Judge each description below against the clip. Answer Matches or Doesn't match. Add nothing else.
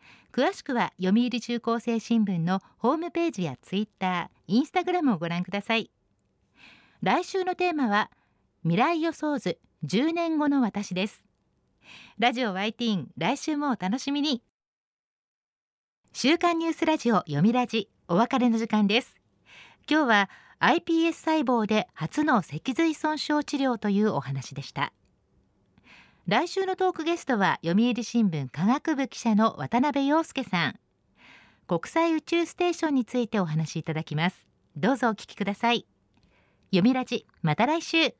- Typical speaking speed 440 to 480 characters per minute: Doesn't match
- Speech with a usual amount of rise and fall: Doesn't match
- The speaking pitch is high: Matches